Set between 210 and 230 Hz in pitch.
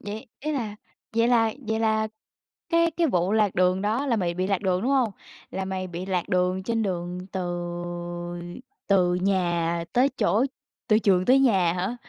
No: high, 200 Hz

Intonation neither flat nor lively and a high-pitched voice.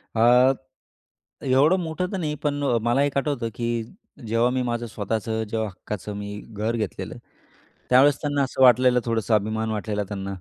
No: average, 3.8 semitones; low, 115 Hz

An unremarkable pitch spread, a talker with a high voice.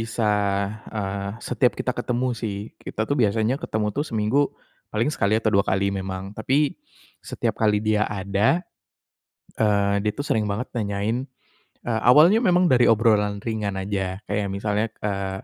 No: average, 3.2 semitones; low, 105 Hz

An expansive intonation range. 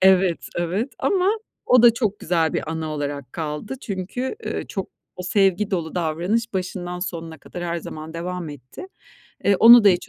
No: average, 4.2 semitones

